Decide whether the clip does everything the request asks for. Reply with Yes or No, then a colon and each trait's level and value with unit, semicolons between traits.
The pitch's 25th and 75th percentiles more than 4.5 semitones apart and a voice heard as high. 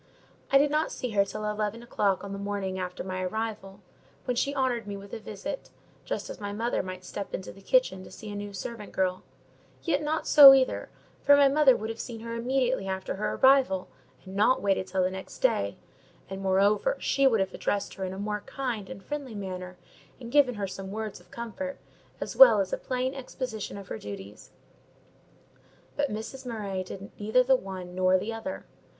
Yes: average, 5.1 semitones; high, 210 Hz